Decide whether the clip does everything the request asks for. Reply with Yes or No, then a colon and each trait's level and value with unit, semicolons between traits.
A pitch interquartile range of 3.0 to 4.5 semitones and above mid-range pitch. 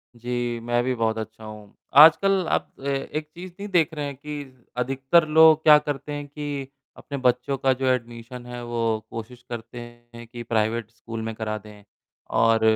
No: average, 4.1 semitones; low, 125 Hz